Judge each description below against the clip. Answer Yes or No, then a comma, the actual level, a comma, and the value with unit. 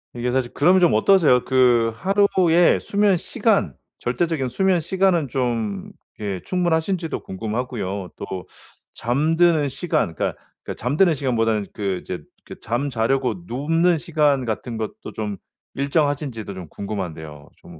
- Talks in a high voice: No, low, 130 Hz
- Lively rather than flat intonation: Yes, wide, 6.9 semitones